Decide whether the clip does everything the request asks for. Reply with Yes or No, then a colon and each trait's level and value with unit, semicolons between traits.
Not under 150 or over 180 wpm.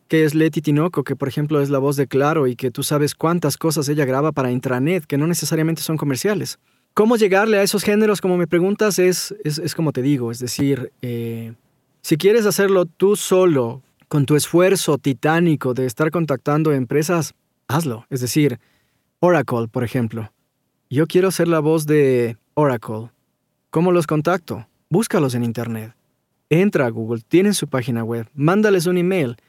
Yes: average, 175 wpm